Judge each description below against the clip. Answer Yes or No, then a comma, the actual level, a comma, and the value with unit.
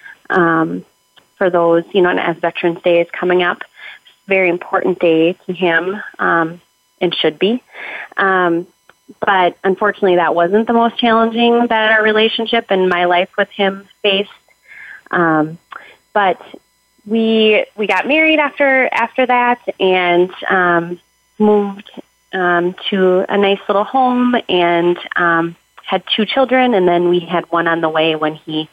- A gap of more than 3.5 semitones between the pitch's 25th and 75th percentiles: Yes, average, 4.4 semitones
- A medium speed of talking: Yes, average, 150 wpm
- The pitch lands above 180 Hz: Yes, high, 190 Hz